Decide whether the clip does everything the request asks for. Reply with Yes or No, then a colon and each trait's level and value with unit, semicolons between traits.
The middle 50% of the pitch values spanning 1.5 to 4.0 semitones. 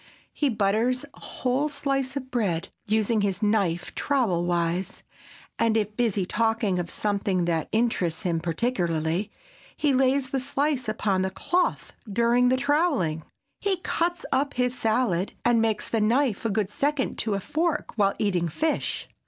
No: wide, 5.6 semitones